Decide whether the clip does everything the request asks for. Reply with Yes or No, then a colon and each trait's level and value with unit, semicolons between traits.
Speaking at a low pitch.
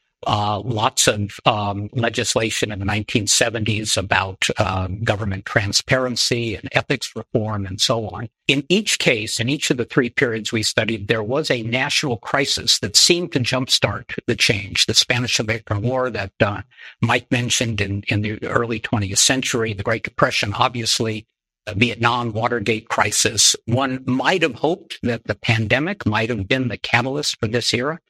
Yes: low, 115 Hz